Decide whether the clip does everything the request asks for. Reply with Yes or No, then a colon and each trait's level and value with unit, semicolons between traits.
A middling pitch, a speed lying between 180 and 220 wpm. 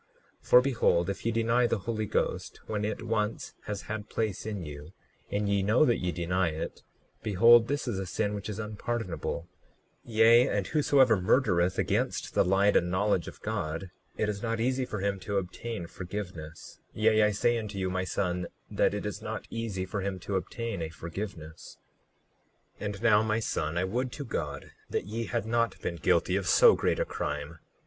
No: low, 105 Hz; average, 195 wpm